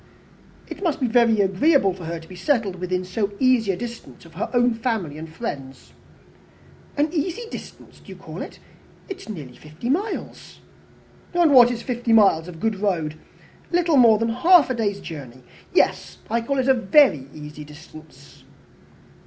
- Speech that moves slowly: No, average, 175 wpm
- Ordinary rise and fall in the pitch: No, wide, 7.6 semitones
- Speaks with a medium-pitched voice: No, high, 215 Hz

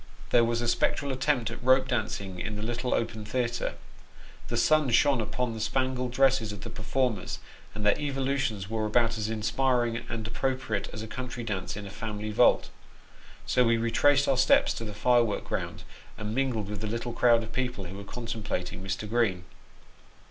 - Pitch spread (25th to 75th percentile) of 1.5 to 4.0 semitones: Yes, average, 3.1 semitones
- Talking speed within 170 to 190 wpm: Yes, average, 185 wpm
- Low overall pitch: Yes, low, 115 Hz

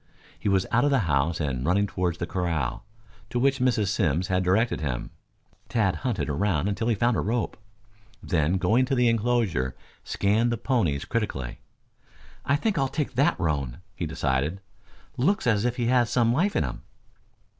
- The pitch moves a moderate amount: No, wide, 6.5 semitones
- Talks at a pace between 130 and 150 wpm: No, average, 175 wpm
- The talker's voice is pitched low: Yes, low, 105 Hz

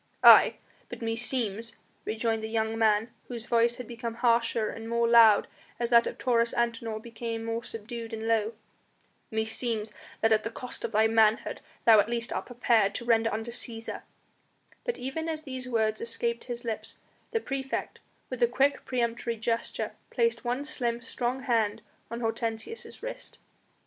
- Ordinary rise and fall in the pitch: No, narrow, 1.3 semitones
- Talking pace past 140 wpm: Yes, average, 165 wpm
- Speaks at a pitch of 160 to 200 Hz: No, high, 230 Hz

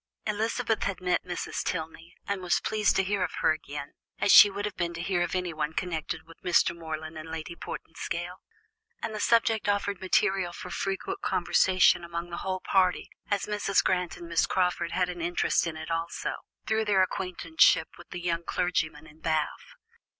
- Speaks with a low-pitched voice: No, medium, 180 Hz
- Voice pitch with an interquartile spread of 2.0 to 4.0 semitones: Yes, average, 2.7 semitones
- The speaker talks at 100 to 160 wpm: No, average, 185 wpm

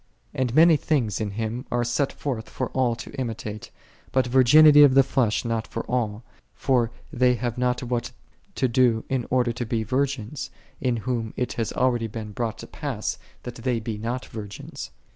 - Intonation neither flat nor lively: No, narrow, 2.3 semitones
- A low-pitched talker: Yes, low, 120 Hz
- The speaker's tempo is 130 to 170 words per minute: No, average, 180 wpm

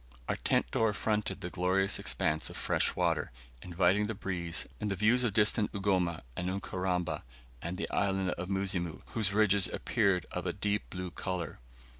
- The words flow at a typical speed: Yes, average, 170 wpm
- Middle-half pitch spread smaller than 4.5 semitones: Yes, narrow, 2.4 semitones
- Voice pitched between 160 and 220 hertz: No, very low, 95 Hz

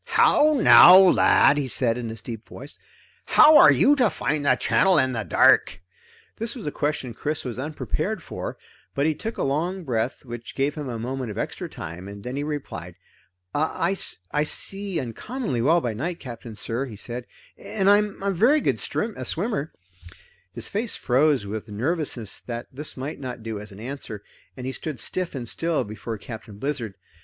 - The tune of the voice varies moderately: No, wide, 6.3 semitones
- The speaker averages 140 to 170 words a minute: No, average, 185 wpm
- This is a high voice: No, low, 135 Hz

